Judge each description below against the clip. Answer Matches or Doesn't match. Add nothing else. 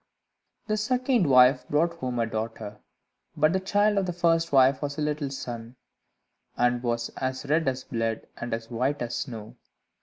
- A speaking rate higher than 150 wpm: Matches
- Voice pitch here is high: Doesn't match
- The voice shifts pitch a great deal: Matches